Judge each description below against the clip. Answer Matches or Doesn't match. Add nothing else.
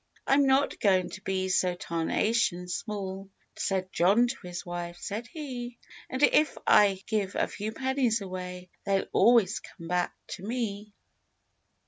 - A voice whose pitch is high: Matches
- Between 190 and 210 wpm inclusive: Doesn't match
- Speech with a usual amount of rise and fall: Matches